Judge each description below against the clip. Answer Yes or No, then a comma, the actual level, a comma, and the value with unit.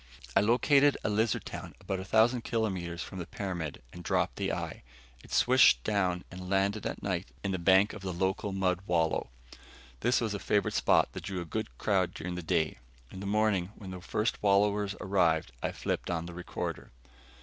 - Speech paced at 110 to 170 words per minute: No, average, 195 wpm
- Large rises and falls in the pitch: No, average, 2.7 semitones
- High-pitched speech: No, very low, 95 Hz